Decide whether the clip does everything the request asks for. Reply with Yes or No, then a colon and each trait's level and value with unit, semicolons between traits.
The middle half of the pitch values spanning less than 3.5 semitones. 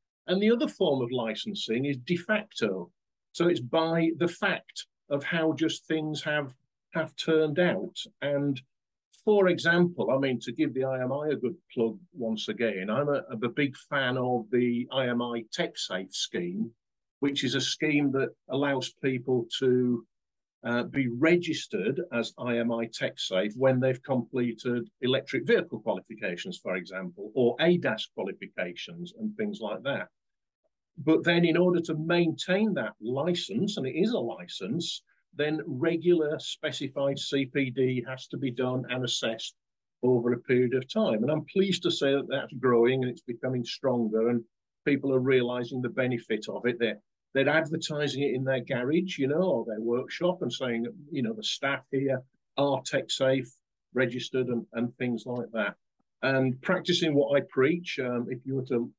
No: average, 4.7 semitones